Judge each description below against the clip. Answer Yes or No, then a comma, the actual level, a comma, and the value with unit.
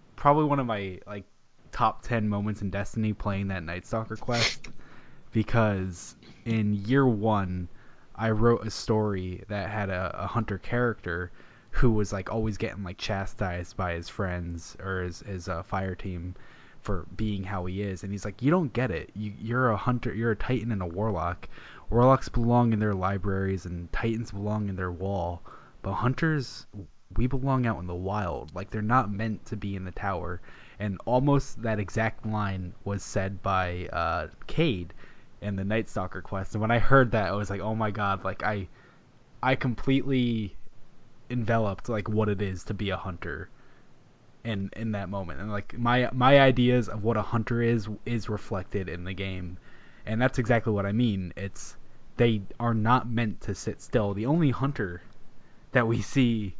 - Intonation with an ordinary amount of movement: Yes, average, 3.4 semitones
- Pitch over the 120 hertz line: No, low, 105 Hz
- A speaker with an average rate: Yes, average, 185 wpm